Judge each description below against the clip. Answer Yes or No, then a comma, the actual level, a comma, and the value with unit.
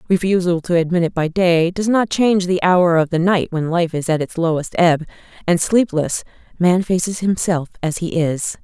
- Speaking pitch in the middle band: Yes, medium, 175 Hz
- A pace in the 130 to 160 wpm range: No, average, 200 wpm